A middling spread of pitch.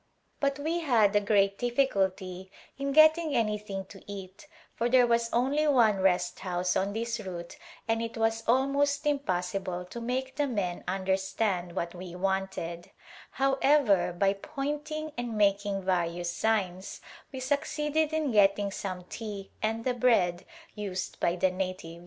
No: wide, 5.8 semitones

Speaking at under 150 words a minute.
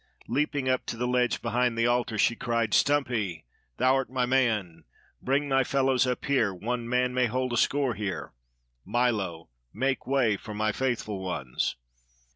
No: average, 160 wpm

